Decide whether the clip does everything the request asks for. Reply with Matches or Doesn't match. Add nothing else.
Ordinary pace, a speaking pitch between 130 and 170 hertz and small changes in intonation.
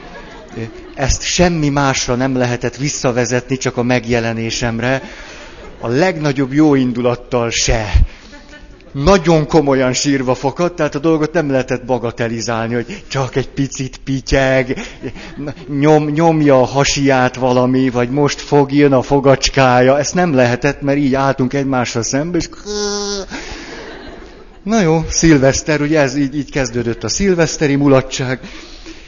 Doesn't match